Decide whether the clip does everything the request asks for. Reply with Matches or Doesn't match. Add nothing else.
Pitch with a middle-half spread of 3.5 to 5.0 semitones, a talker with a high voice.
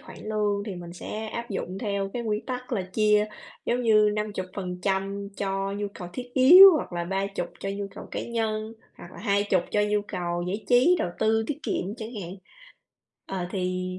Doesn't match